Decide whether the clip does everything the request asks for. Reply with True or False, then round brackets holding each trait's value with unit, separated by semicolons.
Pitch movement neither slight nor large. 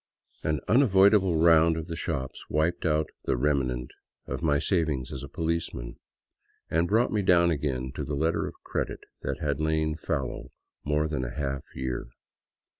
True (3.3 semitones)